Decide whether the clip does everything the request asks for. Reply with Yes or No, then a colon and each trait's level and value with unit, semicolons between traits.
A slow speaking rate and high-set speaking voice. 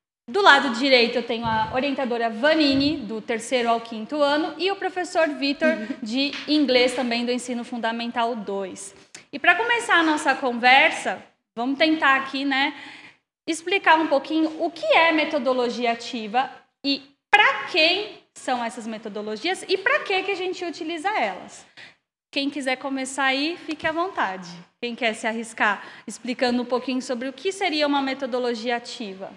No: average, 155 wpm; very high, 270 Hz